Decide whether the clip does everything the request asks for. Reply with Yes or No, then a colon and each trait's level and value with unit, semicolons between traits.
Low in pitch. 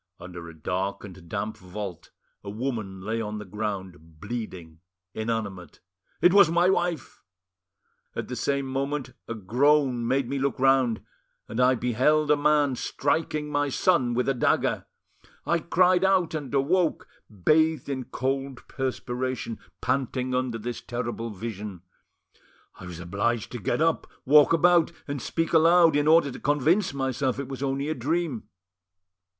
Yes: low, 130 Hz